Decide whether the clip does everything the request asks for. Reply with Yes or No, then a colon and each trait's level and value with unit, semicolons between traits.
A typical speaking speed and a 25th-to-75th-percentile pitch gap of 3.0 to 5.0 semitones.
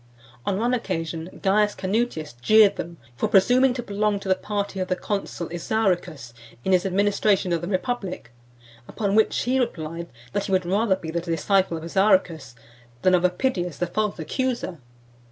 Yes: average, 170 wpm; average, 3.5 semitones